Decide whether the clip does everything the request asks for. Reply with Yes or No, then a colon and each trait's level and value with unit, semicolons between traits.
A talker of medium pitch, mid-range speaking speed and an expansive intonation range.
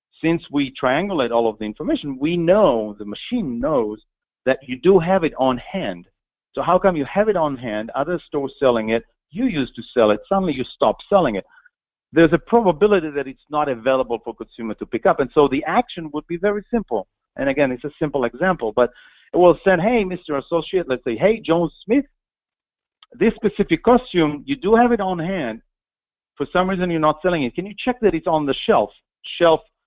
No: medium, 165 Hz; fast, 210 wpm; wide, 7.1 semitones